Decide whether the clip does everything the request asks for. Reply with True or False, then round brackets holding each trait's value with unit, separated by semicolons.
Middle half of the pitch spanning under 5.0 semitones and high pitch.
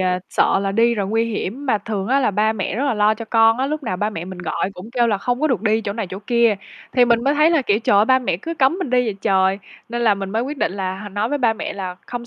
True (3.8 semitones; 225 Hz)